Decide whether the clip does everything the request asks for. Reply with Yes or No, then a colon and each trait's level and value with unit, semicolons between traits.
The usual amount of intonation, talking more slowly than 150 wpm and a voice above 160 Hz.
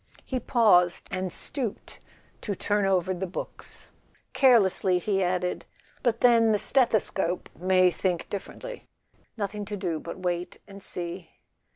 Yes: average, 3.1 semitones; average, 140 wpm; high, 190 Hz